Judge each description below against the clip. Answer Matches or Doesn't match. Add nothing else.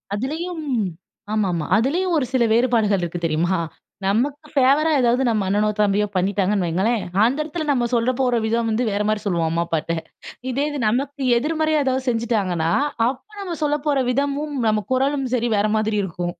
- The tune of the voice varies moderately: Doesn't match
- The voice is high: Matches